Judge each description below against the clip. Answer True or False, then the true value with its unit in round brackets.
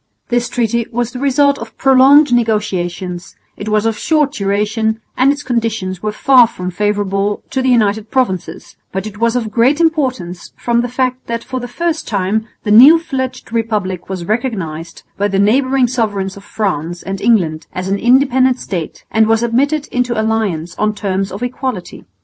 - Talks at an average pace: True (175 wpm)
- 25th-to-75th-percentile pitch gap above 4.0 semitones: True (4.4 semitones)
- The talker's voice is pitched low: False (225 Hz)